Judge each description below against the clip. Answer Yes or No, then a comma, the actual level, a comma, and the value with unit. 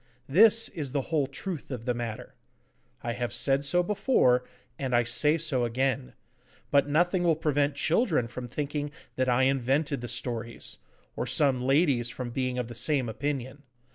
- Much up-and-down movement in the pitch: No, average, 3.4 semitones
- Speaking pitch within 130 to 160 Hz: Yes, low, 135 Hz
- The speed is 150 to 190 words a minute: Yes, average, 170 wpm